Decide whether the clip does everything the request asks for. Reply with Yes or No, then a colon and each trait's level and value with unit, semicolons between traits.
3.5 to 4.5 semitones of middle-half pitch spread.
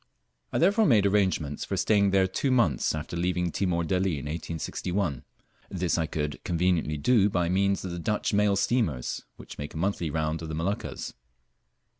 Yes: average, 3.8 semitones